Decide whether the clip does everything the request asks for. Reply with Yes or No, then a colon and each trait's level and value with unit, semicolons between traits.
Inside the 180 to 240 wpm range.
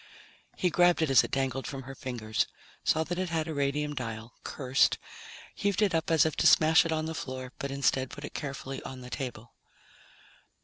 Yes: fast, 205 wpm